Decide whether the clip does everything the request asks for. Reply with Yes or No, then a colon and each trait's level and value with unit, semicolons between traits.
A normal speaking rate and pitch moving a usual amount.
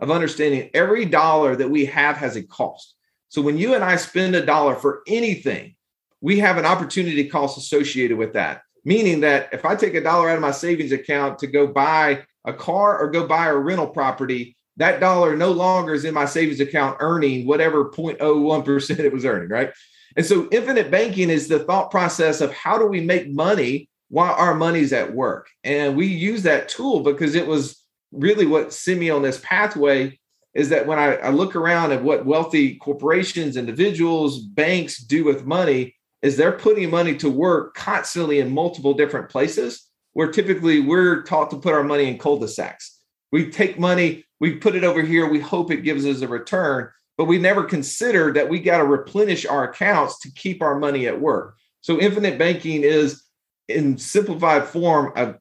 Yes: average, 195 wpm; average, 3.5 semitones